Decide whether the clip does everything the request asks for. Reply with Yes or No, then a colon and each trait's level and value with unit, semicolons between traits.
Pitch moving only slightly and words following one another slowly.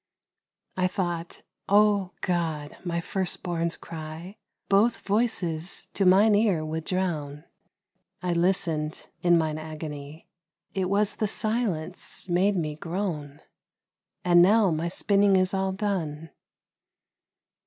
No: average, 3.6 semitones; slow, 115 wpm